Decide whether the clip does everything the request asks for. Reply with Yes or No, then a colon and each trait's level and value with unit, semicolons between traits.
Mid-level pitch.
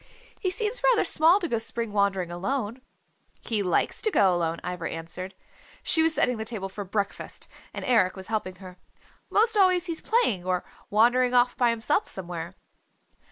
No: high, 220 Hz